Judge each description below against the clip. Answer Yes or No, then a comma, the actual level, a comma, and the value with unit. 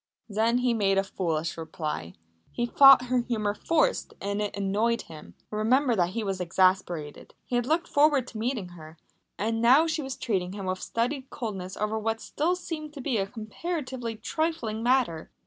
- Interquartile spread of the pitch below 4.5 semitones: No, average, 5.1 semitones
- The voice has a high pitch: Yes, high, 225 Hz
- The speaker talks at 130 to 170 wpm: No, average, 180 wpm